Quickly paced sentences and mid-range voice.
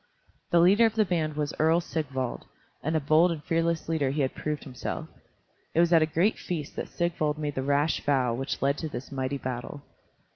Yes: fast, 210 wpm; medium, 155 Hz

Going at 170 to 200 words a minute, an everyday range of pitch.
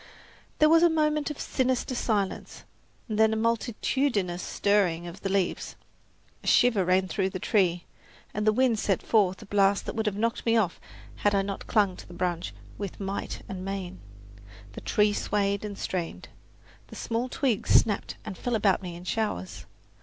Yes: average, 175 wpm; average, 3.3 semitones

